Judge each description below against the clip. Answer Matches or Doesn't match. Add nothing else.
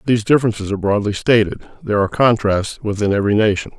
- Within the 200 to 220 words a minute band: Doesn't match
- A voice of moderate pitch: Doesn't match